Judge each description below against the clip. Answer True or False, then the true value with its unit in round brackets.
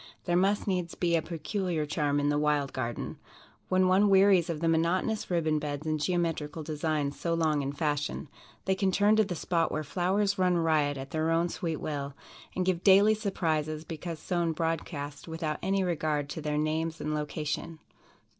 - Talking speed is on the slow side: False (185 wpm)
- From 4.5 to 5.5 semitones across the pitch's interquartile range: False (3.2 semitones)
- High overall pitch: False (165 Hz)